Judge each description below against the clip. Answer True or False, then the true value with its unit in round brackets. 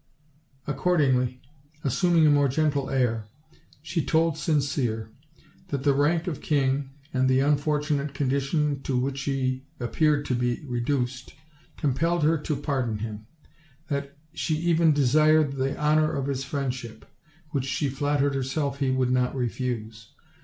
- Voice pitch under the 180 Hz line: True (140 Hz)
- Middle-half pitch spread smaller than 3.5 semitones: True (2.6 semitones)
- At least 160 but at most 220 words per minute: False (145 wpm)